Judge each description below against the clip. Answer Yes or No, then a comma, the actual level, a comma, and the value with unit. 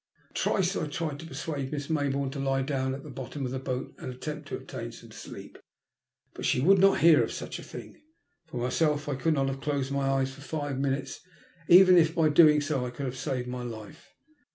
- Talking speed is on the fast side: Yes, fast, 225 wpm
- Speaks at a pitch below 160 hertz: Yes, medium, 140 Hz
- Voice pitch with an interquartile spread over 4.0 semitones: No, narrow, 2.6 semitones